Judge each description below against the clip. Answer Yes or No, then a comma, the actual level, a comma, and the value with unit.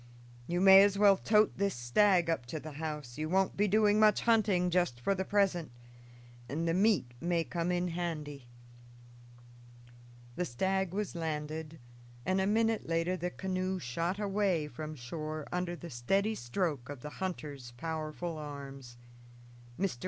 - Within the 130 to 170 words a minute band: Yes, average, 155 wpm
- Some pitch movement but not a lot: Yes, average, 4.2 semitones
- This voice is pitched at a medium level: Yes, medium, 175 Hz